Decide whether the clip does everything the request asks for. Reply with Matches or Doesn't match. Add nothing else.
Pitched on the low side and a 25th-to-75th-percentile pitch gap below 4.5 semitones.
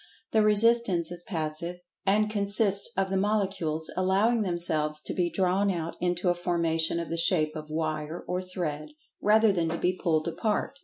Doesn't match